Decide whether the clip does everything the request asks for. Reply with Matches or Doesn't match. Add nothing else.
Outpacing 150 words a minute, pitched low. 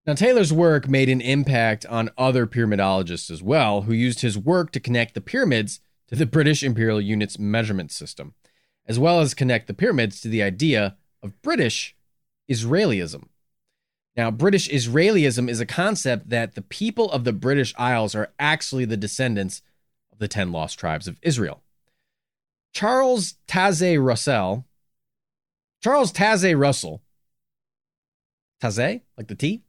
Doesn't match